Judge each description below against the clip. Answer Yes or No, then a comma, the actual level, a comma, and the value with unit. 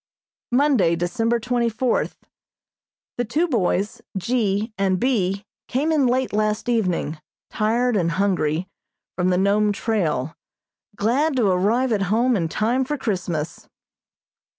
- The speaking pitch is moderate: No, high, 215 Hz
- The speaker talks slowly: Yes, slow, 130 wpm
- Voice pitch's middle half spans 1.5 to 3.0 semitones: No, average, 4.9 semitones